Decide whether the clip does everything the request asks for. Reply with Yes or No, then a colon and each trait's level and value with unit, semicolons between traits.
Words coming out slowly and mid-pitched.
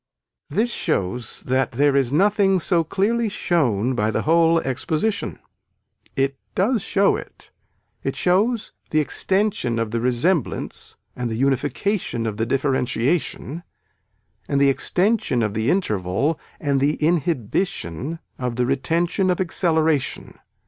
Yes: slow, 130 wpm; medium, 145 Hz